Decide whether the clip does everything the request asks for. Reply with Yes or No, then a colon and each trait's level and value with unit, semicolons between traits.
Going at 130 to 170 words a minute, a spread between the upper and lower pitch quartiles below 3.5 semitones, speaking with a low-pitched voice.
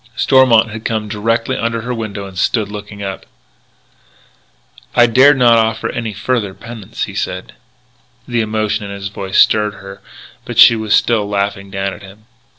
Yes: average, 160 wpm; narrow, 2.5 semitones; low, 110 Hz